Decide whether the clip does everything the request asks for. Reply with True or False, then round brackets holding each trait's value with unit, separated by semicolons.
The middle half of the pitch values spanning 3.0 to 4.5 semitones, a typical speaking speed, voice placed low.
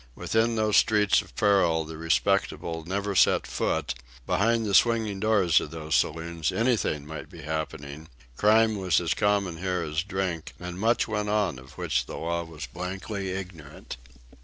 True (4.2 semitones; 160 wpm; 90 Hz)